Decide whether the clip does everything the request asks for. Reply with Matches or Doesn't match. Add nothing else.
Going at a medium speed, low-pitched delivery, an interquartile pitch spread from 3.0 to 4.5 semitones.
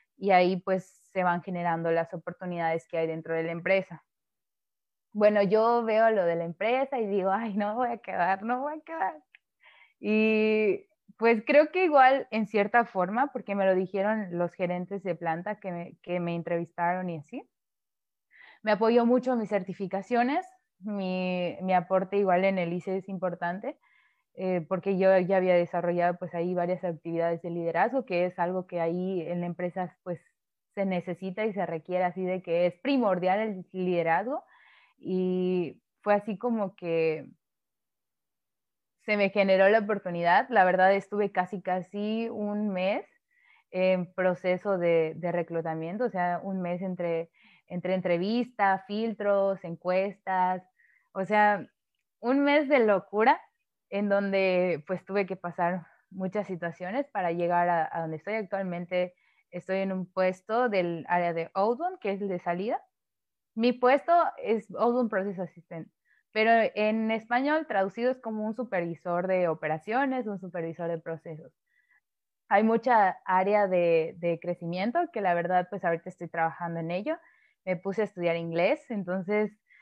Doesn't match